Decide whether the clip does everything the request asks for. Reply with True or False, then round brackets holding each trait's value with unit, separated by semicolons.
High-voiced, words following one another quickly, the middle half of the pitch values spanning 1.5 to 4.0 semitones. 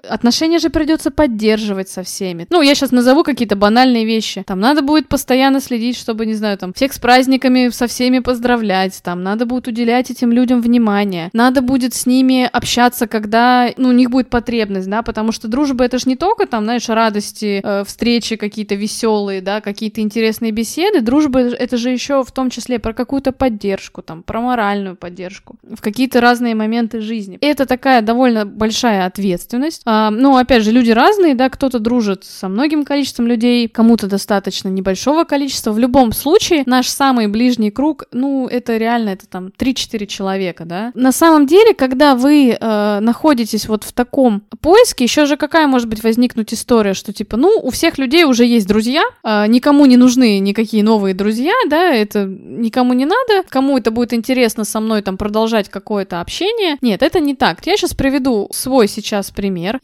True (240 Hz; 180 wpm; 3.5 semitones)